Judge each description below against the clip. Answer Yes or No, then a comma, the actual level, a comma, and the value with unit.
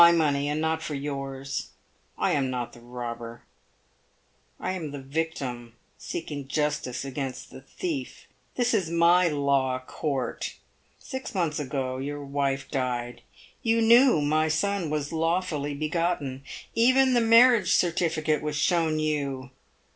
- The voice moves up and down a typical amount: Yes, average, 3.9 semitones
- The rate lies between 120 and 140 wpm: Yes, slow, 135 wpm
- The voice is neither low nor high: Yes, medium, 150 Hz